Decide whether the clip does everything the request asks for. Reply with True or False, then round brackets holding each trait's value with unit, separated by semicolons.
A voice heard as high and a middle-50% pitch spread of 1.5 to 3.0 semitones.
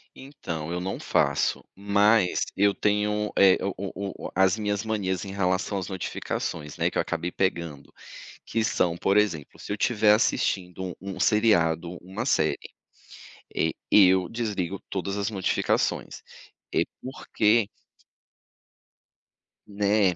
False (100 Hz; 2.6 semitones)